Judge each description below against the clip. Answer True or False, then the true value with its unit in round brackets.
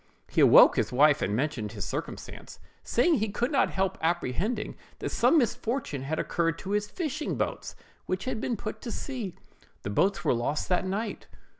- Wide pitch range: True (7.6 semitones)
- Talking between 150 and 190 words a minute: True (175 wpm)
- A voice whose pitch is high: True (195 Hz)